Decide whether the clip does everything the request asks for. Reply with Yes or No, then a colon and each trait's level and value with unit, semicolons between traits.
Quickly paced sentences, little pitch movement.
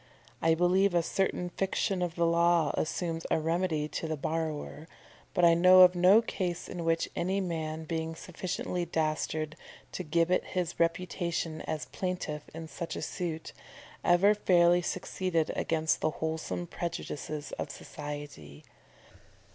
No: average, 140 wpm; narrow, 2.1 semitones